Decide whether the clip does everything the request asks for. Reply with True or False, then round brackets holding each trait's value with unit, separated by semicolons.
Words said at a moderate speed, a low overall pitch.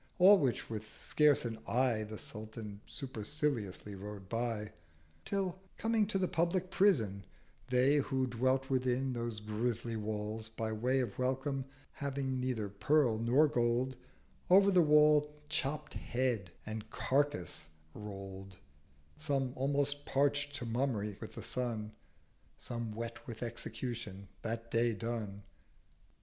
False (130 wpm; 120 Hz)